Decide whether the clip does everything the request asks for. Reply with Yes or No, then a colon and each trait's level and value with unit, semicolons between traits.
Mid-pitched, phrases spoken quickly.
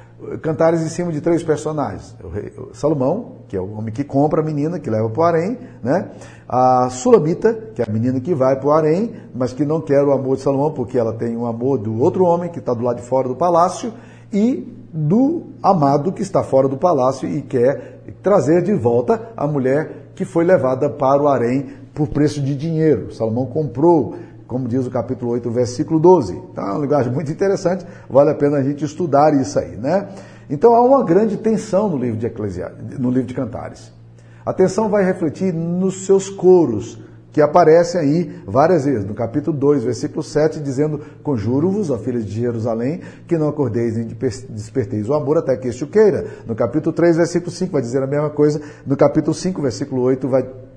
Yes: medium, 145 Hz; fast, 205 wpm